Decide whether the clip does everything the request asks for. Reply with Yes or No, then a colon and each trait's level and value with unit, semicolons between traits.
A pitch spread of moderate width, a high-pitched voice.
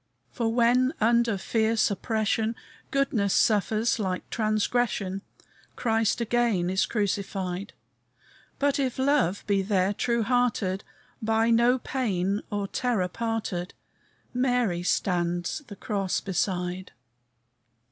Yes: average, 3.7 semitones; high, 215 Hz